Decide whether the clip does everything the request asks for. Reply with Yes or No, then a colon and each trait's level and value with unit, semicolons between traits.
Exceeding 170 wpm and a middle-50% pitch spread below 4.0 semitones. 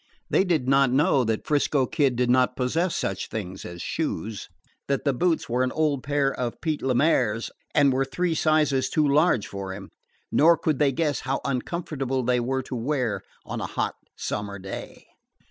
Yes: average, 185 wpm; average, 3.6 semitones